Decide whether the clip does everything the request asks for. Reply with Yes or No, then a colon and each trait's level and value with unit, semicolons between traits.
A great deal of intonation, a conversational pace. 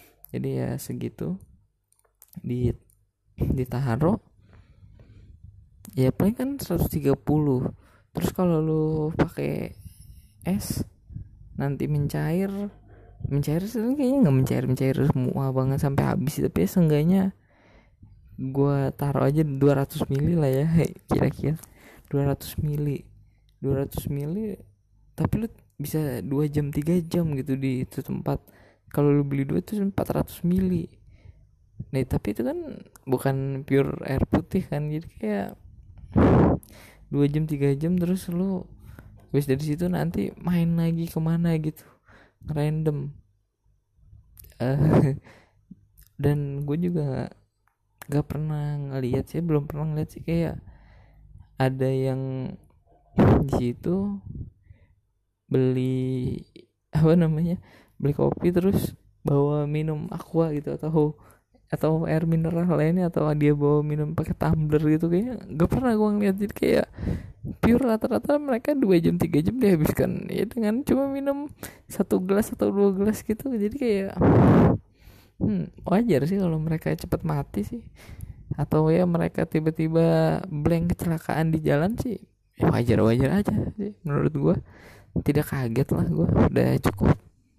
Yes: wide, 6.1 semitones; average, 125 wpm